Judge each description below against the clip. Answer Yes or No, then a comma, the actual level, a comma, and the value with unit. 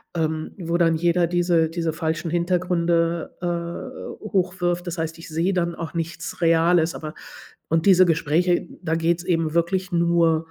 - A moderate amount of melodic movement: No, narrow, 1.3 semitones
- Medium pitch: Yes, medium, 170 Hz